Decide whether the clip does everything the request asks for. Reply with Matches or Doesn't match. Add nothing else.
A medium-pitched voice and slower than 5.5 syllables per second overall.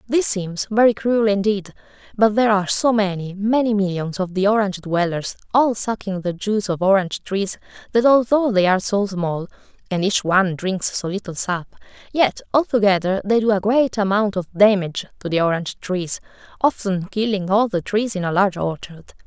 Doesn't match